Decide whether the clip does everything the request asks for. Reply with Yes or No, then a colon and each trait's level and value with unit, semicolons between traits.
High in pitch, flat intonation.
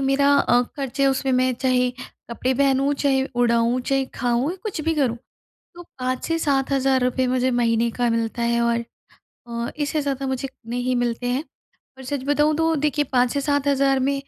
Yes: very high, 265 Hz; narrow, 2.3 semitones